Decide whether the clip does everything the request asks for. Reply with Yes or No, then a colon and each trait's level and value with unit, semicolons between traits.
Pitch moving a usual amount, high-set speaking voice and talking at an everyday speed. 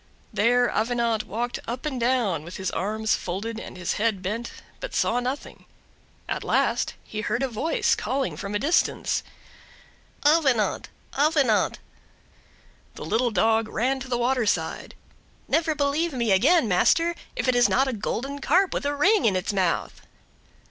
Yes: average, 4.5 semitones; high, 240 Hz; average, 155 wpm